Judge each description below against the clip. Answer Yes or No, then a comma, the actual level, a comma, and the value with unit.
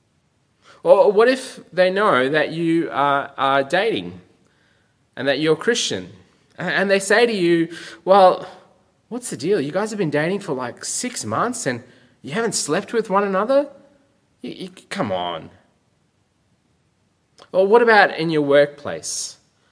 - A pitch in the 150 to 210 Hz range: Yes, medium, 185 Hz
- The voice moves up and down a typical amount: No, wide, 7.8 semitones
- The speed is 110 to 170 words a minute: Yes, average, 150 wpm